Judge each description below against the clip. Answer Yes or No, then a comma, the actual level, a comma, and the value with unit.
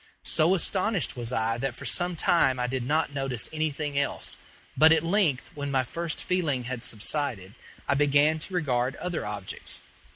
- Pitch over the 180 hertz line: No, medium, 145 Hz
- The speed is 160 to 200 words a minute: Yes, average, 170 wpm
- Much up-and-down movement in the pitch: No, average, 4.3 semitones